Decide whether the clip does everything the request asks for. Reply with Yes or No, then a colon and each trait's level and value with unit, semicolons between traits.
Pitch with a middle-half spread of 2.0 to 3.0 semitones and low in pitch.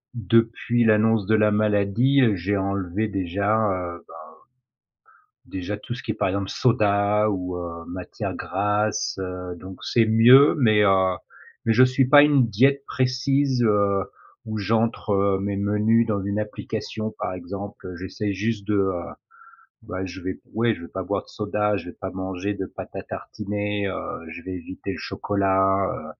Yes: average, 2.7 semitones; low, 100 Hz